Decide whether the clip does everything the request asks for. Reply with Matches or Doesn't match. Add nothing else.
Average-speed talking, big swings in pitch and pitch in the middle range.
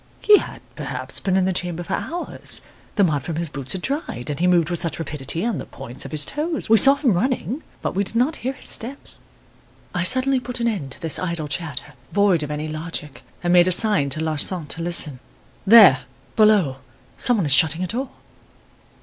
Doesn't match